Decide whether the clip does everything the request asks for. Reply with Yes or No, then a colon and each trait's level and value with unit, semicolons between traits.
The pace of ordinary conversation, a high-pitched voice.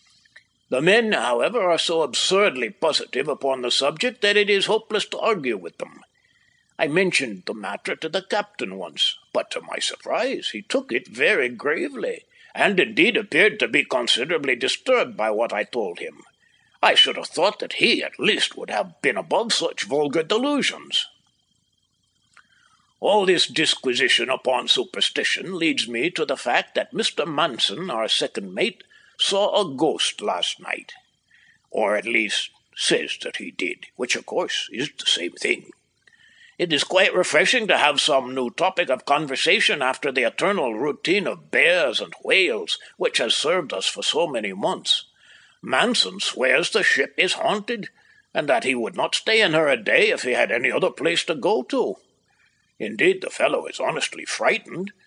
Yes: average, 170 wpm; very high, 365 Hz